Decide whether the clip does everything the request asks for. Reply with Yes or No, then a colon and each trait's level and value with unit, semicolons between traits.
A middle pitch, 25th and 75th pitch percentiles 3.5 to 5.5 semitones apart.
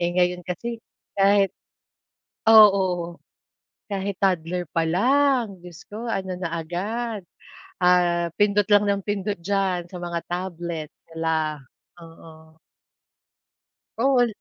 No: medium, 180 Hz; average, 3.0 semitones